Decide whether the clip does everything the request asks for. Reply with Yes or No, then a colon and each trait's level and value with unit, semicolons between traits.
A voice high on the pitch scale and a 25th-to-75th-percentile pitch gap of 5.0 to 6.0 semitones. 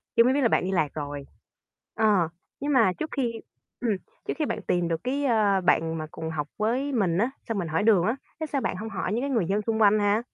Yes: high, 210 Hz; average, 5.3 semitones